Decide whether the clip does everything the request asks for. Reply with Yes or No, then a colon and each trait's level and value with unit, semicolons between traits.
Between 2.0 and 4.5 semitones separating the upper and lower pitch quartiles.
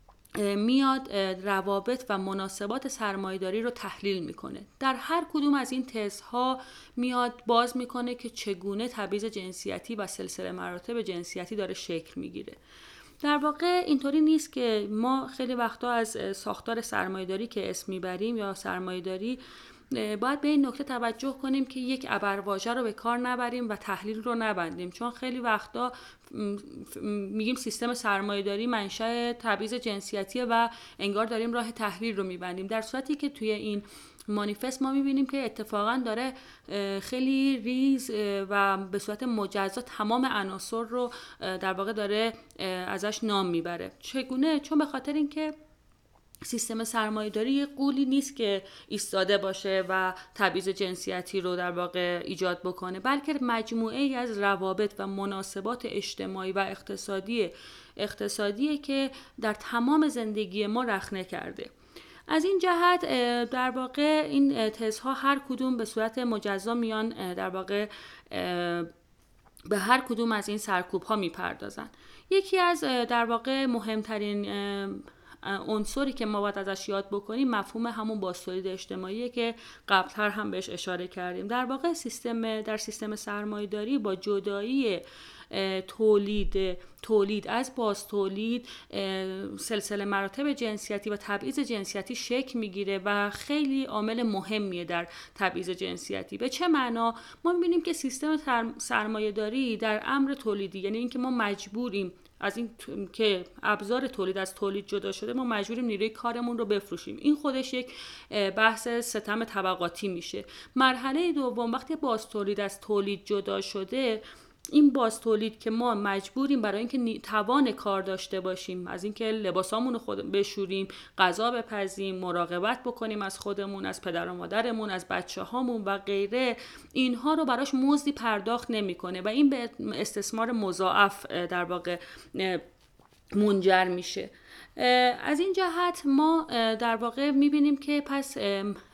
Yes: average, 4.1 semitones